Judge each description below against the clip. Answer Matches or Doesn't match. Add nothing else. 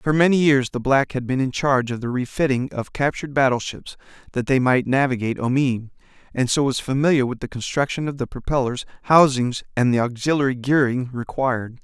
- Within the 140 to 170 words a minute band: Doesn't match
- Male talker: Matches